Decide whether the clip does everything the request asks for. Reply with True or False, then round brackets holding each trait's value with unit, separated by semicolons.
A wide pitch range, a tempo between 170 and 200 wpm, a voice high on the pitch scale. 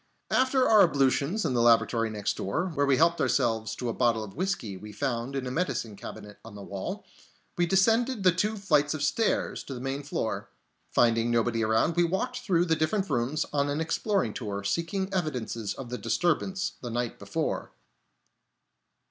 False (7.8 semitones; 180 wpm; 140 Hz)